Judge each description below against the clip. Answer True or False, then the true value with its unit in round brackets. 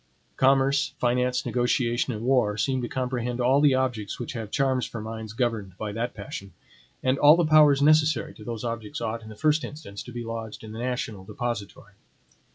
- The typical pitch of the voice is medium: False (120 Hz)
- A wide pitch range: False (3.2 semitones)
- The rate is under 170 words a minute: False (190 wpm)